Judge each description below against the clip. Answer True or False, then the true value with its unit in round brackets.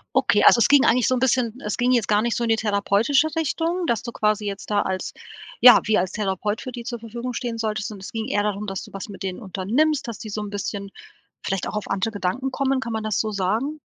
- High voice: True (220 Hz)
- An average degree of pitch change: True (3.3 semitones)